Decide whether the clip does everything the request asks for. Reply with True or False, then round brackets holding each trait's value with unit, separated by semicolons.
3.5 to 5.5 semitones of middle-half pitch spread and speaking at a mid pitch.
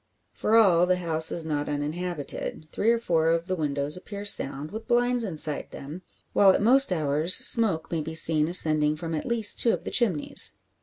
True (4.9 semitones; 170 Hz)